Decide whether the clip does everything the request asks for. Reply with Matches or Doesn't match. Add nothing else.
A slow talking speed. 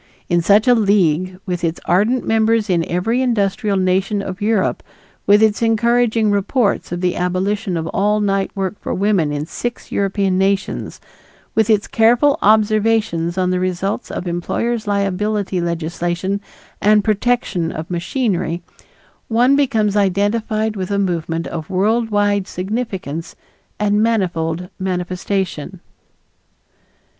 Matches